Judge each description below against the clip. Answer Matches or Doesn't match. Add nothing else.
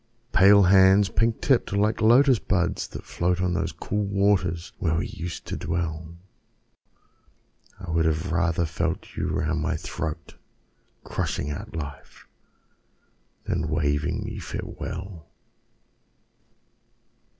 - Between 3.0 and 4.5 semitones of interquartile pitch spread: Matches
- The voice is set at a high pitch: Doesn't match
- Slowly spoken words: Matches